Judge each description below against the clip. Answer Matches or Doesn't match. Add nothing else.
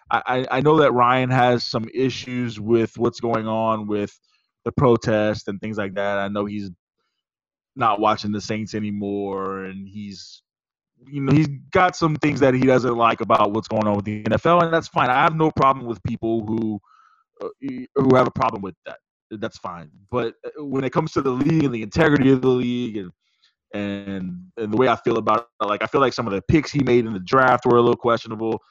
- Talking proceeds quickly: Matches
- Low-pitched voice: Matches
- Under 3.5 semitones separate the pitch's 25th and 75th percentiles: Doesn't match